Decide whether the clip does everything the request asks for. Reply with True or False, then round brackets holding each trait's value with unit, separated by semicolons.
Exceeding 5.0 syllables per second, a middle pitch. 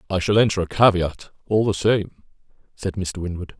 False (5.2 syllables/s; 95 Hz)